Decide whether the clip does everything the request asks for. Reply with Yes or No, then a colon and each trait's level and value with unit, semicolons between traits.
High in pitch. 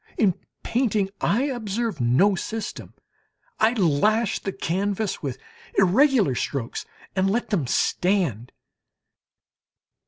Yes: high, 200 Hz